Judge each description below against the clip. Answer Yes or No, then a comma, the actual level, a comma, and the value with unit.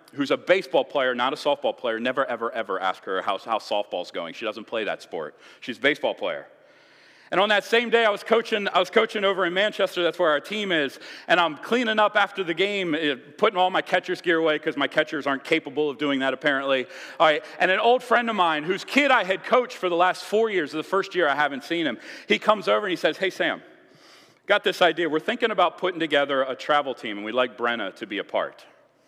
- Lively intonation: Yes, wide, 5.7 semitones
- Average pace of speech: No, fast, 245 wpm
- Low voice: No, medium, 180 Hz